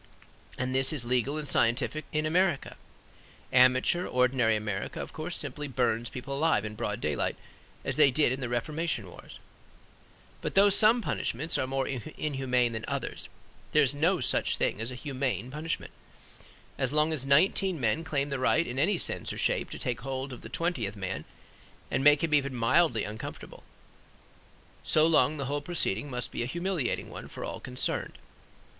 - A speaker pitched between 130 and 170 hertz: Yes, low, 135 Hz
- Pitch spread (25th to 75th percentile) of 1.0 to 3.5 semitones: No, average, 4.0 semitones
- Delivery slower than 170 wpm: No, average, 175 wpm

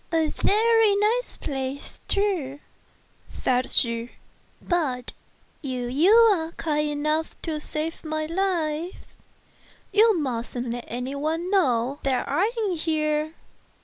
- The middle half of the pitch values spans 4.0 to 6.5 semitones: Yes, average, 5.2 semitones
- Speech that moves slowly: Yes, slow, 130 wpm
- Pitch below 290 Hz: No, very high, 310 Hz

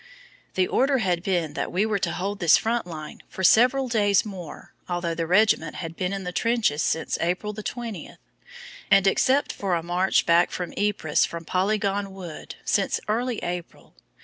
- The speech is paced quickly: No, average, 175 wpm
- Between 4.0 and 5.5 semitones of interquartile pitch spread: No, average, 3.5 semitones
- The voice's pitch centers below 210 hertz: Yes, high, 190 Hz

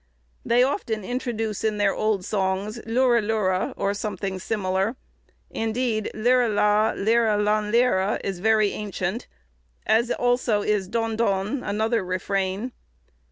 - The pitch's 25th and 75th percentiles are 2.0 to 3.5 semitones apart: Yes, average, 2.8 semitones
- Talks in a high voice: Yes, high, 215 Hz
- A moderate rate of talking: No, slow, 115 wpm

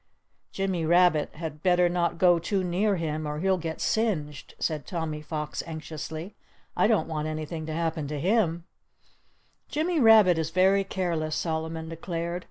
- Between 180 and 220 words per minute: No, average, 155 wpm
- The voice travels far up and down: No, average, 2.8 semitones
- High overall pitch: No, medium, 165 Hz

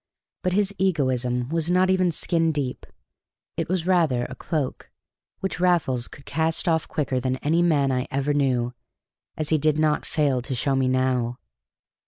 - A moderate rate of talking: Yes, average, 170 wpm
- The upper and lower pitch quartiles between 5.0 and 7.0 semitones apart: No, average, 4.5 semitones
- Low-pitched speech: No, medium, 150 Hz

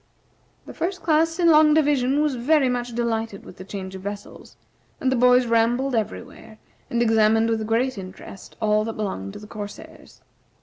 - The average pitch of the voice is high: Yes, high, 230 Hz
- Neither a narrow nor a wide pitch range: Yes, average, 3.9 semitones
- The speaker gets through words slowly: No, average, 175 wpm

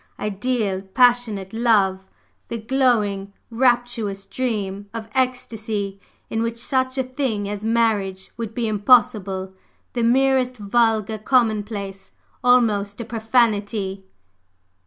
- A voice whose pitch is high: Yes, high, 220 Hz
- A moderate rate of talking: No, slow, 105 wpm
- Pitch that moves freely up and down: No, average, 3.3 semitones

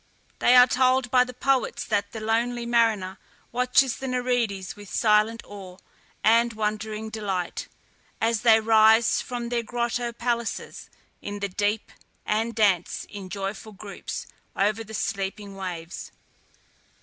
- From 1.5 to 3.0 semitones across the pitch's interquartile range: Yes, average, 2.7 semitones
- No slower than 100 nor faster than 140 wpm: Yes, slow, 135 wpm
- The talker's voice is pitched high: Yes, high, 220 Hz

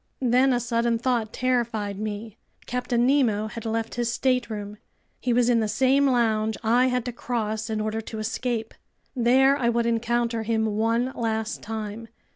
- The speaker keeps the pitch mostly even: Yes, narrow, 2.1 semitones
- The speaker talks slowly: No, average, 165 wpm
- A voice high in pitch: Yes, high, 230 Hz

